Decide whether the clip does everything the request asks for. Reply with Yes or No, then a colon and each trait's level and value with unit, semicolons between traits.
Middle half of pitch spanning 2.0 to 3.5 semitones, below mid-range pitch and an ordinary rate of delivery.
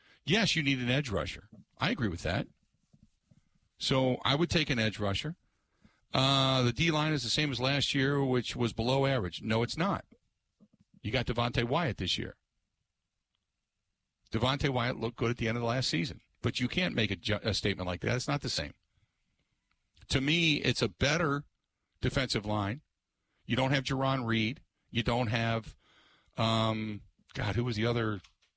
No: average, 3.9 semitones; low, 120 Hz; average, 180 wpm